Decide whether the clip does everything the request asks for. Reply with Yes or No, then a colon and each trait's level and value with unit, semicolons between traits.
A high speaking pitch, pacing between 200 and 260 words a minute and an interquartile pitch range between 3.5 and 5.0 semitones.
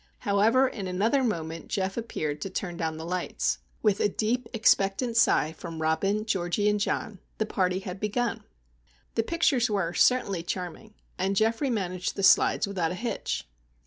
No: high, 200 Hz; average, 165 wpm; average, 3.8 semitones